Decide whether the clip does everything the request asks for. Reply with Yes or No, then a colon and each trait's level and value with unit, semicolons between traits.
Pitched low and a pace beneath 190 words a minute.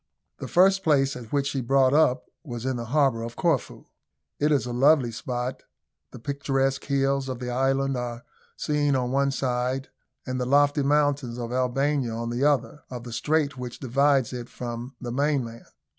Yes: low, 130 Hz; average, 180 wpm